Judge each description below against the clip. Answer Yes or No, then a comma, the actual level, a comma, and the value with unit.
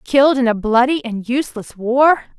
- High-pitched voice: Yes, very high, 250 Hz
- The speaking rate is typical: Yes, average, 175 wpm